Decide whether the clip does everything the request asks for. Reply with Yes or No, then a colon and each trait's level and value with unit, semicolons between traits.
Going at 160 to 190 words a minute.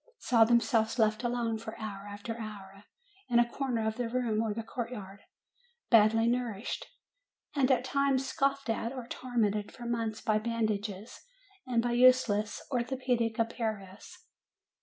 No: average, 150 wpm